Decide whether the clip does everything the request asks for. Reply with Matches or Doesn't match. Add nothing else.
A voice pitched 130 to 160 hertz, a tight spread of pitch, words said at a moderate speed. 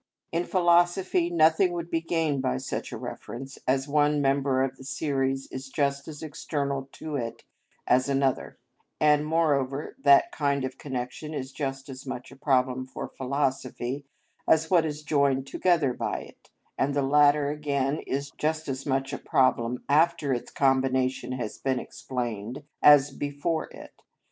Matches